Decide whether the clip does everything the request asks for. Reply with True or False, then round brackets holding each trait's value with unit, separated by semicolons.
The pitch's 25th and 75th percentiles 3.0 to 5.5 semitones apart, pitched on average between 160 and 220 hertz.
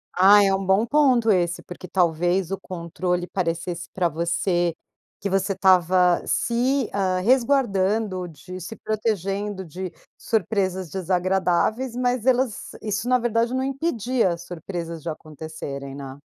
True (4.2 semitones; 190 Hz)